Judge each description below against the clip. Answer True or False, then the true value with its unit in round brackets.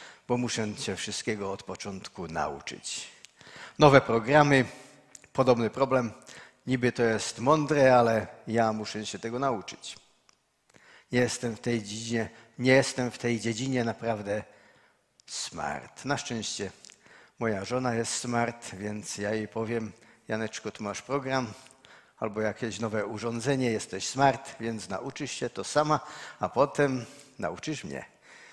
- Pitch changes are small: False (3.2 semitones)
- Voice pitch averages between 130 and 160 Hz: False (120 Hz)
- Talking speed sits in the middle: True (130 wpm)